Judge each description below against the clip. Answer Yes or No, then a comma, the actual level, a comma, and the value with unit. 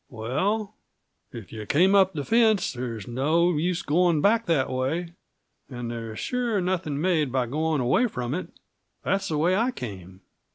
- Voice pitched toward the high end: No, medium, 155 Hz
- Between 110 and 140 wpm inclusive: No, average, 165 wpm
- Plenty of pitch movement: Yes, wide, 7.1 semitones